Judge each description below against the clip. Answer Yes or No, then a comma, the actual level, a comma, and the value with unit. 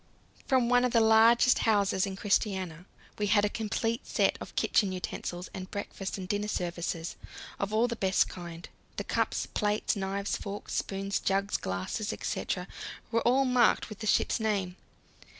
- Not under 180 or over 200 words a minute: No, average, 165 wpm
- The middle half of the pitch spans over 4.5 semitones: No, average, 2.8 semitones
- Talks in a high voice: Yes, high, 205 Hz